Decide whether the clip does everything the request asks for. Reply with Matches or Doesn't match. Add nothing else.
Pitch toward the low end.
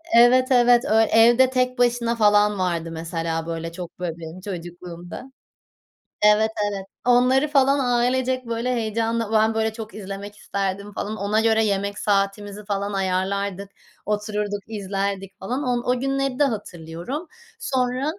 Doesn't match